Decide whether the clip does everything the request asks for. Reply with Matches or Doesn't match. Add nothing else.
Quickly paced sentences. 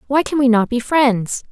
Matches